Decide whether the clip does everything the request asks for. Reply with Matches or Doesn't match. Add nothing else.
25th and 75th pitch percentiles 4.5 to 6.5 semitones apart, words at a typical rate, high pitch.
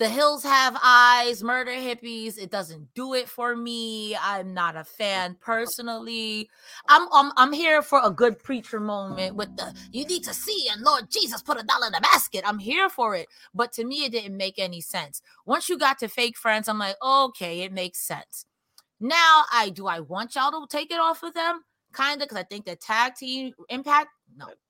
Doesn't match